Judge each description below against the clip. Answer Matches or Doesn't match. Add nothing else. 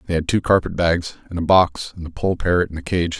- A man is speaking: Matches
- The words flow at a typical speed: Doesn't match